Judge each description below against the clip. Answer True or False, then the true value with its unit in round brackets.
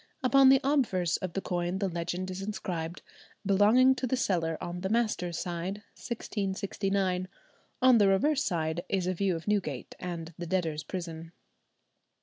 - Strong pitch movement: False (3.2 semitones)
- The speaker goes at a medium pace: True (155 wpm)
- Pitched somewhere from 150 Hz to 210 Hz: True (185 Hz)